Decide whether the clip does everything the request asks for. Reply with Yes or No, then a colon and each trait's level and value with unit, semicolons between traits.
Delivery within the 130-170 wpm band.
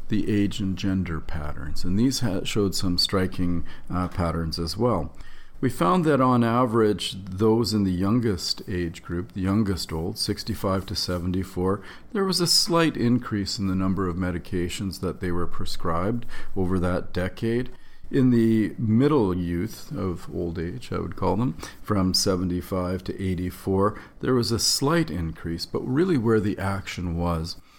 Yes: average, 160 wpm